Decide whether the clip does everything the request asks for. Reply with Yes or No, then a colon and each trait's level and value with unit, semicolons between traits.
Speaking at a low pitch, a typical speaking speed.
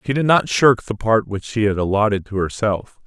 No: low, 110 Hz; fast, 235 wpm